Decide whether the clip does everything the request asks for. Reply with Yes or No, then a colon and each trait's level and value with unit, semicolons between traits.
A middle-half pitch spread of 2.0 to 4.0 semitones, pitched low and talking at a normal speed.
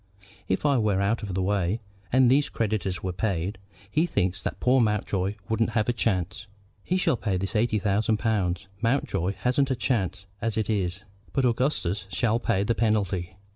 Yes: average, 3.5 semitones; low, 105 Hz; average, 180 wpm